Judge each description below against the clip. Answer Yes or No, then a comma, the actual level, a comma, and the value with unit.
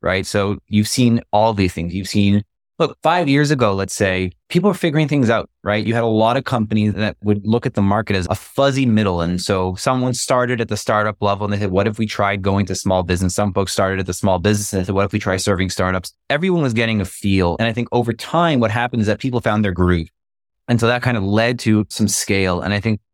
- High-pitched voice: No, low, 105 Hz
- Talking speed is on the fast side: Yes, fast, 265 wpm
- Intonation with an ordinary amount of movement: Yes, average, 3.2 semitones